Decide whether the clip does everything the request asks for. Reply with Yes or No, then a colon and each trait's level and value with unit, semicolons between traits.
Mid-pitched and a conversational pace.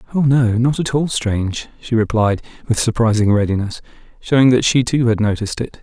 No: low, 115 Hz; average, 185 wpm